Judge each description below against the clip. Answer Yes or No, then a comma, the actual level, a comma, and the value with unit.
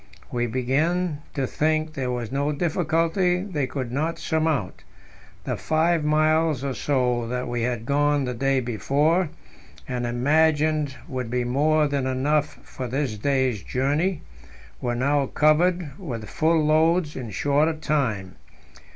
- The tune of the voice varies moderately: Yes, average, 3.8 semitones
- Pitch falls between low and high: Yes, medium, 145 Hz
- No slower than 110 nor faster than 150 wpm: Yes, average, 140 wpm